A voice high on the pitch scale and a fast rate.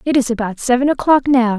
Yes: very high, 250 Hz; fast, 225 wpm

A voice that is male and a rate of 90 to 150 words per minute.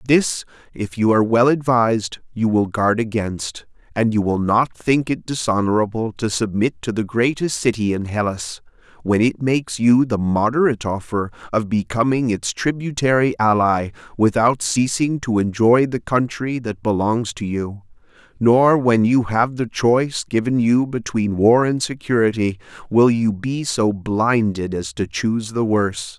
No: male; average, 160 wpm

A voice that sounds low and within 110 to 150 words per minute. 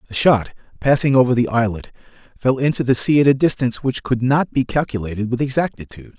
No: low, 125 Hz; average, 195 wpm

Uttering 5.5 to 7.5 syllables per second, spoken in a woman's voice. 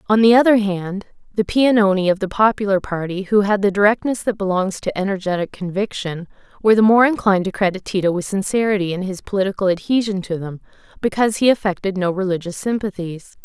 Yes: 6.2 syllables/s; female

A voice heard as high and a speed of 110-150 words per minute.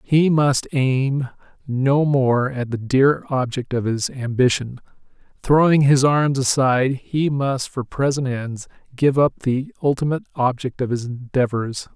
No: low, 135 Hz; average, 145 wpm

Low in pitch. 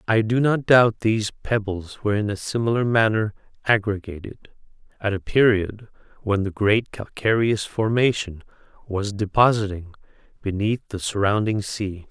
Yes: low, 105 Hz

